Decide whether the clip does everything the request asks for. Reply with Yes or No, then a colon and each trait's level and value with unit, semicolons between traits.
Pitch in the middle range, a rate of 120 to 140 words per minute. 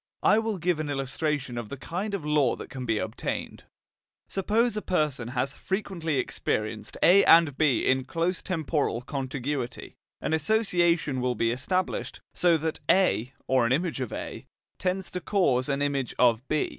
No: medium, 150 Hz; average, 170 wpm